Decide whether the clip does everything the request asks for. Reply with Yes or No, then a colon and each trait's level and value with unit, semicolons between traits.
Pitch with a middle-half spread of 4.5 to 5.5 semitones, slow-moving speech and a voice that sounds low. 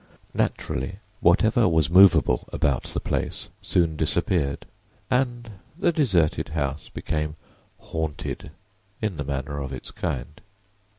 Yes: average, 5.2 semitones; slow, 115 wpm; very low, 80 Hz